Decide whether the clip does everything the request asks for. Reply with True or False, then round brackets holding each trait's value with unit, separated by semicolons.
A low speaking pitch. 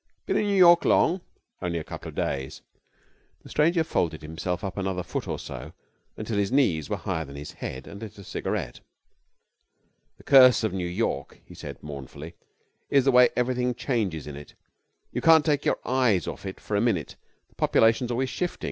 True (105 Hz)